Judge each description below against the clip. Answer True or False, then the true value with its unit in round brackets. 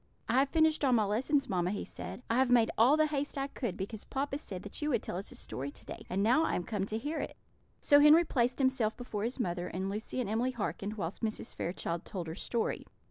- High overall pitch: True (230 Hz)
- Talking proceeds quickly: True (250 wpm)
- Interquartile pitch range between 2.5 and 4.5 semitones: False (5.4 semitones)